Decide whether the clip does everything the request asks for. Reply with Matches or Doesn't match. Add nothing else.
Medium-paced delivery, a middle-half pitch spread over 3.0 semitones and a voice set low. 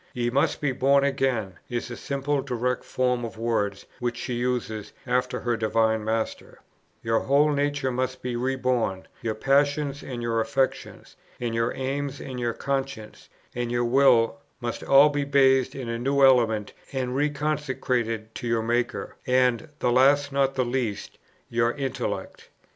Doesn't match